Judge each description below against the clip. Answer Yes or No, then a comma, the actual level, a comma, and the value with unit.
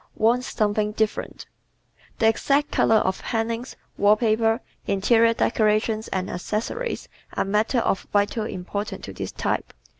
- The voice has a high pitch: Yes, high, 220 Hz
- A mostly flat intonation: Yes, narrow, 1.6 semitones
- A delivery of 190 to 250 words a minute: No, average, 140 wpm